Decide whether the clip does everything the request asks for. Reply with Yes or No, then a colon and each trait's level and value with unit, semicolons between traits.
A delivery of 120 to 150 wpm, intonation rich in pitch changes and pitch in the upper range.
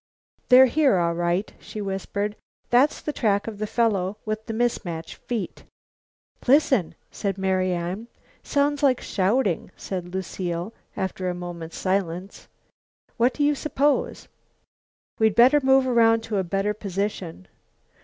No: slow, 135 wpm; average, 4.8 semitones; high, 205 Hz